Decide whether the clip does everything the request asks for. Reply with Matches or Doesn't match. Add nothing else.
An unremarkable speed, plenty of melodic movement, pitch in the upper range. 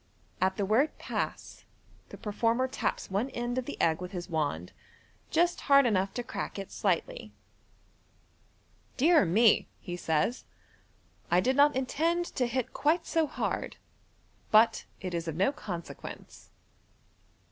Matches